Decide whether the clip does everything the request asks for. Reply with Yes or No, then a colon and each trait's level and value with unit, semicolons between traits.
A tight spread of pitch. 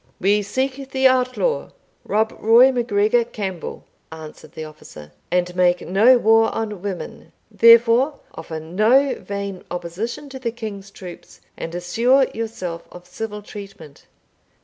No: average, 5.1 semitones